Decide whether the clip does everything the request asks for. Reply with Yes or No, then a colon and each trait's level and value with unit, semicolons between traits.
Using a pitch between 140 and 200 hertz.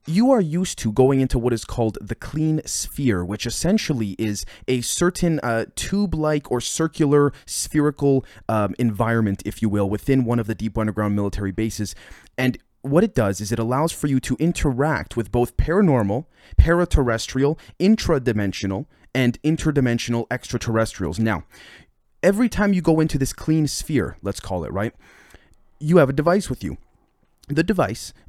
No: low, 125 Hz